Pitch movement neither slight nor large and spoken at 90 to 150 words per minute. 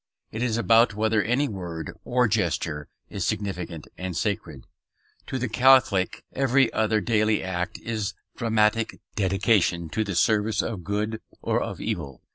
Yes: average, 3.7 semitones; average, 145 wpm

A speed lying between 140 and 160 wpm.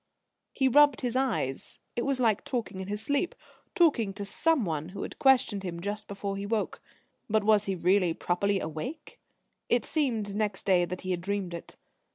No: average, 185 wpm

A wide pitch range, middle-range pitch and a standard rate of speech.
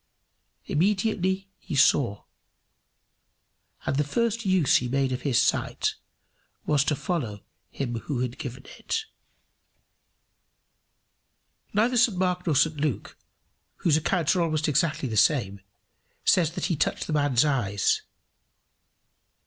No: wide, 5.7 semitones; medium, 150 Hz; slow, 125 wpm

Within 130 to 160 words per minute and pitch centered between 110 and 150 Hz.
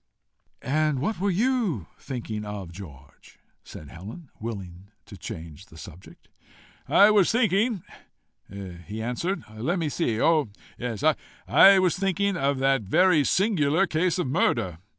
Yes: slow, 135 wpm; medium, 140 Hz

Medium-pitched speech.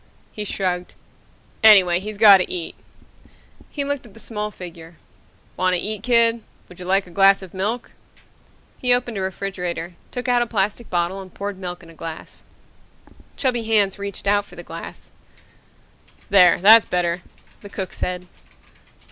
No: high, 195 Hz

